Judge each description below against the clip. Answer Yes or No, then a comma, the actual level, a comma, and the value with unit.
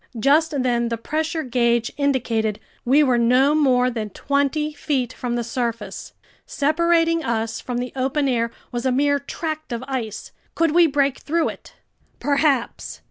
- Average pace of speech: Yes, average, 155 wpm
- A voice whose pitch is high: Yes, very high, 265 Hz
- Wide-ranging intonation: No, average, 3.9 semitones